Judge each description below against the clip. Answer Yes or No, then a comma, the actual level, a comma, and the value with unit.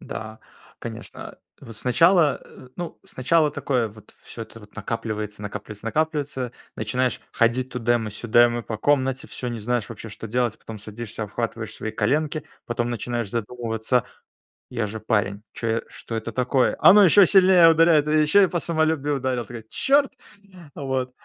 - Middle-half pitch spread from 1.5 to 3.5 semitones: No, average, 4.7 semitones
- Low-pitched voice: Yes, low, 120 Hz